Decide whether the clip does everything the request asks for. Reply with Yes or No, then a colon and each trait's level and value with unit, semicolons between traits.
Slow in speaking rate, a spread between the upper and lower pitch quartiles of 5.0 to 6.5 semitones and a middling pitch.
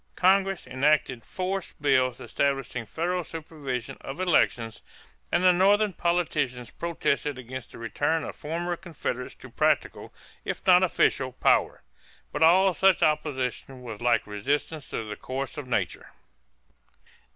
Yes: slow, 130 wpm; wide, 5.5 semitones; medium, 145 Hz